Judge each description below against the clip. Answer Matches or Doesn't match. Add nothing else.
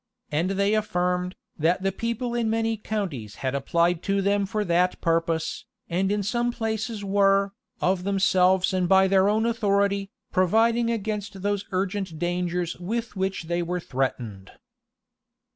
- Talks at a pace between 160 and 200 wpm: Doesn't match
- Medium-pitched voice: Doesn't match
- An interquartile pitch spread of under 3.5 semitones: Matches